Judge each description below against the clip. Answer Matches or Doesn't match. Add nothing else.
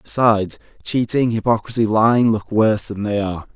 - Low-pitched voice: Matches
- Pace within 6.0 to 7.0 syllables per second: Doesn't match